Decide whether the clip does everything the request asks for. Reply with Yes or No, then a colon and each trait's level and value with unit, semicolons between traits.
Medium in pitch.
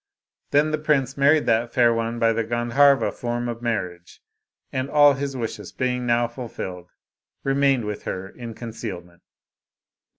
No: low, 120 Hz